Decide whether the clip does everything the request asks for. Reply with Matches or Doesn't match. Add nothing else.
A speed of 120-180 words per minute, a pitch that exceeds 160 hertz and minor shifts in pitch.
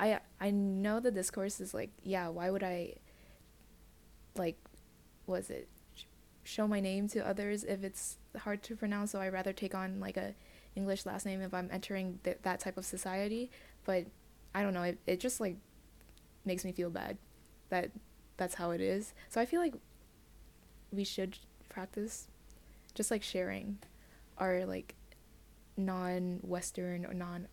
Matches